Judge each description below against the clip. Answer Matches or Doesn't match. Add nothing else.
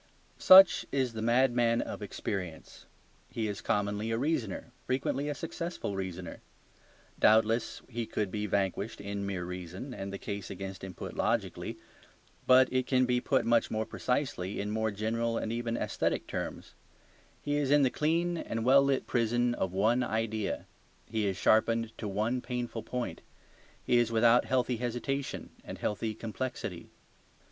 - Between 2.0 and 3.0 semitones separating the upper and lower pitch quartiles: Doesn't match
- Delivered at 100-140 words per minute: Doesn't match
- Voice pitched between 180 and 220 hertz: Doesn't match